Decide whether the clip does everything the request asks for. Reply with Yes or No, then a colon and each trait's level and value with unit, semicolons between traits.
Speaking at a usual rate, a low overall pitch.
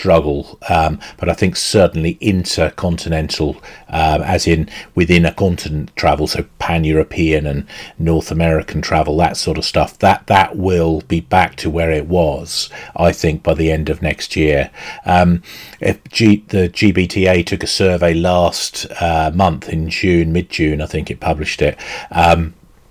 Yes: average, 160 wpm; very low, 85 Hz